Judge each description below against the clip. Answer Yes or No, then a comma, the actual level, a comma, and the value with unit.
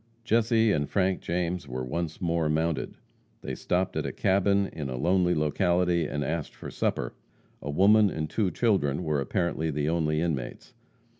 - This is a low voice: Yes, very low, 85 Hz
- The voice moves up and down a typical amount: Yes, average, 3.7 semitones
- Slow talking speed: No, average, 165 wpm